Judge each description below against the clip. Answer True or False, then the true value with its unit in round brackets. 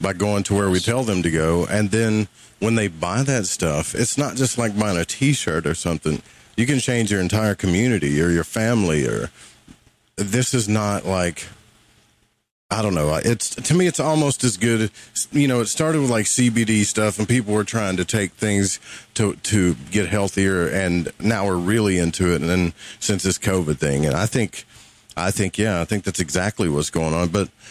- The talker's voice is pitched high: False (105 Hz)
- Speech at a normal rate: False (210 wpm)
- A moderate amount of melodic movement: True (4.1 semitones)